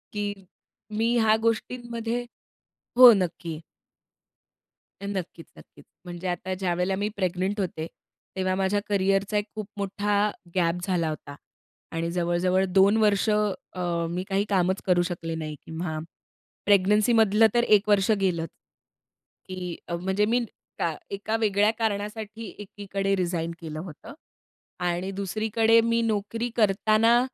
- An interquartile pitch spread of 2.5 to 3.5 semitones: Yes, average, 3.1 semitones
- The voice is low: No, high, 195 Hz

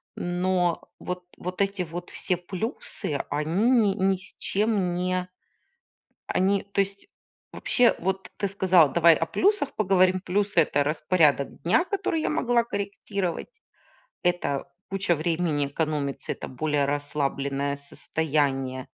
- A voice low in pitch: No, medium, 180 Hz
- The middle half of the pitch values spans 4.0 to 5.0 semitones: Yes, average, 4.6 semitones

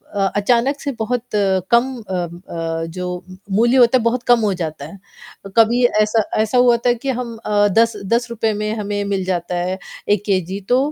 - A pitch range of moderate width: Yes, average, 3.9 semitones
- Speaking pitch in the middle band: No, high, 215 Hz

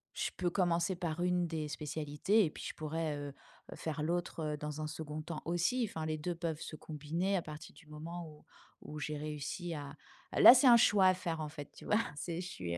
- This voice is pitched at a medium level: Yes, medium, 160 Hz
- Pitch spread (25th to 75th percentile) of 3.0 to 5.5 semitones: No, narrow, 2.6 semitones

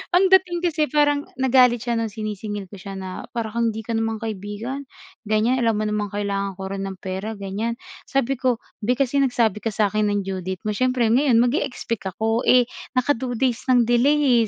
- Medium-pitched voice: No, high, 225 Hz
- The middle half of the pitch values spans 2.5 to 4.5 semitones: Yes, average, 3.6 semitones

